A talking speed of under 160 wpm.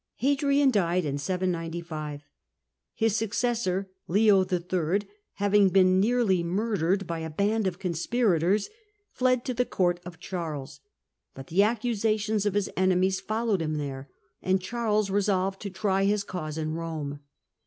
Yes: average, 145 wpm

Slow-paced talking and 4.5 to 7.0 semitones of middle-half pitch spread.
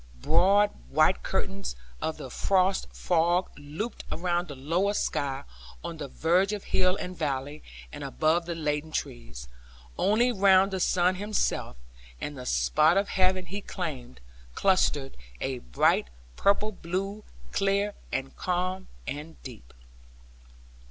Yes: slow, 130 wpm; average, 4.9 semitones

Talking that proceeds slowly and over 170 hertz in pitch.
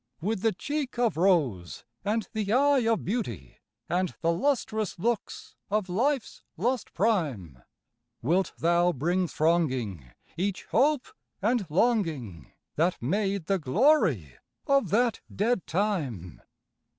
Yes: slow, 120 wpm; high, 190 Hz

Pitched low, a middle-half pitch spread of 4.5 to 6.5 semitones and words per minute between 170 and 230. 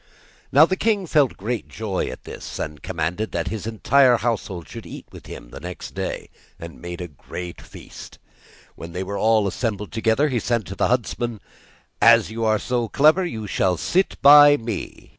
Yes: low, 110 Hz; average, 5.1 semitones; average, 180 wpm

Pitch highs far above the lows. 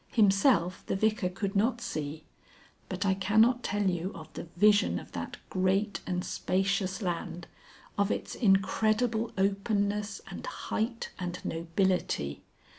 No: average, 2.9 semitones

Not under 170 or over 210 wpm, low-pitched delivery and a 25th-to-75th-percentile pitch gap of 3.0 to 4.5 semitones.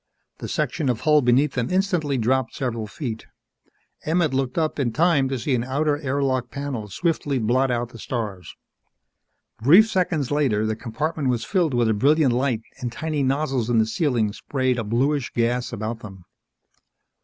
Yes: average, 175 wpm; low, 130 Hz; average, 4.0 semitones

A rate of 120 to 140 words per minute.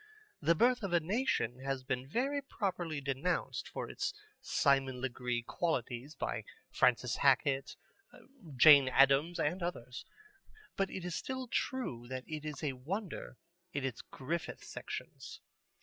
Yes: slow, 135 wpm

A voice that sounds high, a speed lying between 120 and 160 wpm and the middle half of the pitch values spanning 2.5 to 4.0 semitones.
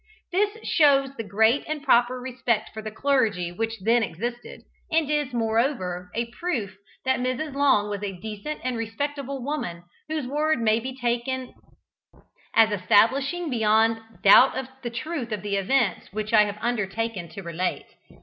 No: high, 235 Hz; average, 155 wpm; average, 4.4 semitones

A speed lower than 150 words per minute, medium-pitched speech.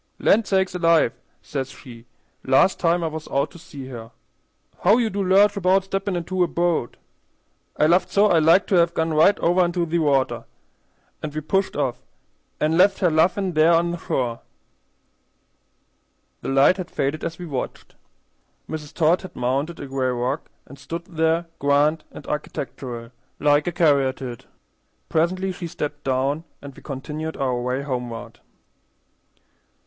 No: average, 160 wpm; medium, 160 Hz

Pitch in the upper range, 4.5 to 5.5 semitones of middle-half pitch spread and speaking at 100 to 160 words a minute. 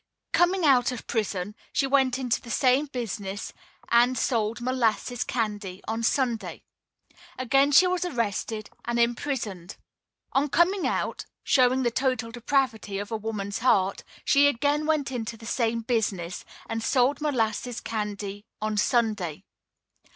No: high, 235 Hz; average, 3.7 semitones; average, 140 wpm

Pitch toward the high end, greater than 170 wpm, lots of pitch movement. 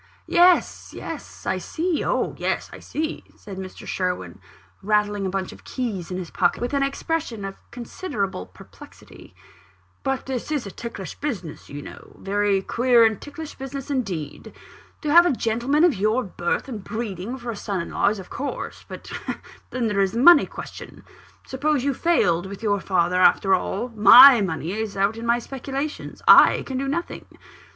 Yes: high, 225 Hz; average, 180 wpm; wide, 5.9 semitones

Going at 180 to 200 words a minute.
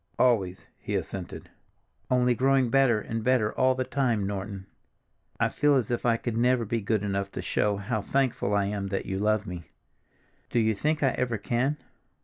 Yes: average, 185 wpm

